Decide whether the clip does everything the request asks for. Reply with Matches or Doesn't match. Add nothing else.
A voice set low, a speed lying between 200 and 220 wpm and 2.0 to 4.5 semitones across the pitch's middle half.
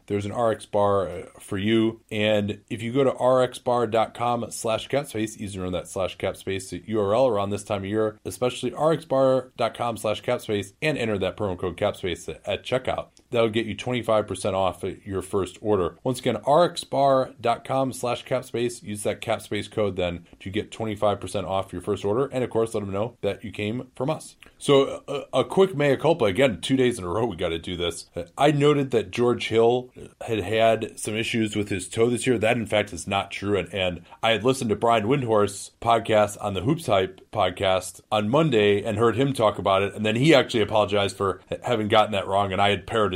Matches